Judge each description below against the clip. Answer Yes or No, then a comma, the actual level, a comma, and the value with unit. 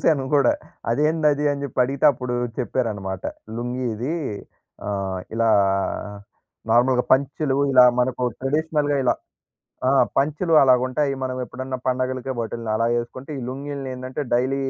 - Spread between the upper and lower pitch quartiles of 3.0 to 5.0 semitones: No, narrow, 2.4 semitones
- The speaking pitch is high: No, low, 130 Hz